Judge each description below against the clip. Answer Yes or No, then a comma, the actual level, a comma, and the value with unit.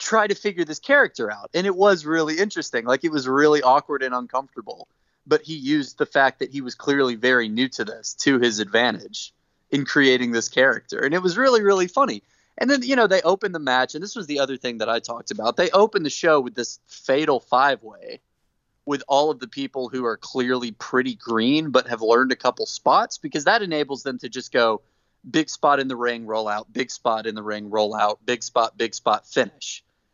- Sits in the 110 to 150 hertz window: Yes, low, 135 Hz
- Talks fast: Yes, fast, 225 wpm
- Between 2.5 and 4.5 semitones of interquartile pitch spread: No, average, 5.2 semitones